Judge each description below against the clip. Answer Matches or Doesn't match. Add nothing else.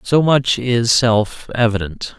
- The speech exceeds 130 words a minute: Doesn't match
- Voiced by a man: Matches